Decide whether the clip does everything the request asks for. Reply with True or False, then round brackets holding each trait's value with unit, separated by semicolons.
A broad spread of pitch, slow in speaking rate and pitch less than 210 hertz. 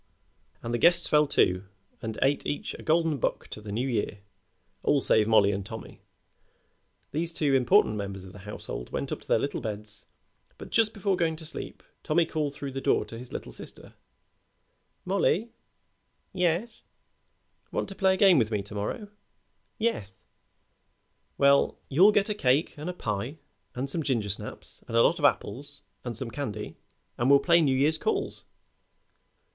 False (7.4 semitones; 175 wpm; 140 Hz)